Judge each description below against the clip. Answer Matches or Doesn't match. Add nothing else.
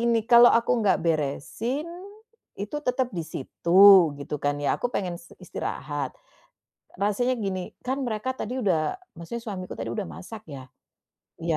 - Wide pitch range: Matches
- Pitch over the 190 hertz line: Matches